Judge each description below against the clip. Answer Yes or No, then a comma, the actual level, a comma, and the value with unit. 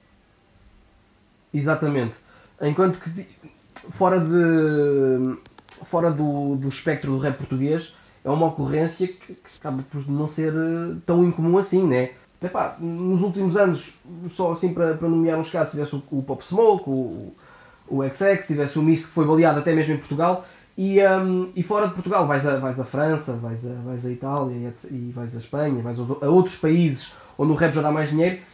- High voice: No, medium, 155 Hz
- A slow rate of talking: No, average, 180 wpm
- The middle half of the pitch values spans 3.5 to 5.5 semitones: Yes, average, 4.3 semitones